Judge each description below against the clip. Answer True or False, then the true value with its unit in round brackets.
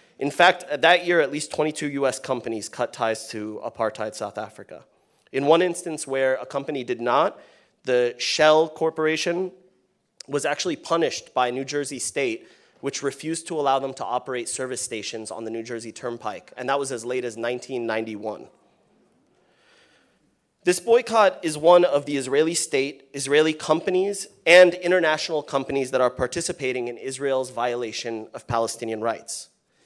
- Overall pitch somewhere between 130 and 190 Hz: True (135 Hz)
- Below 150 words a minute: False (155 wpm)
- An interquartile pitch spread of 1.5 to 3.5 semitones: False (4.8 semitones)